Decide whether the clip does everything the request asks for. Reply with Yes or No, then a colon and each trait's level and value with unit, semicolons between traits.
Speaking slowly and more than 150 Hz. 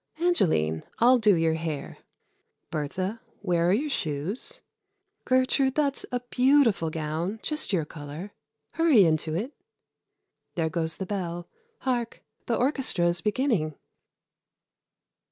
Yes: slow, 120 wpm; high, 190 Hz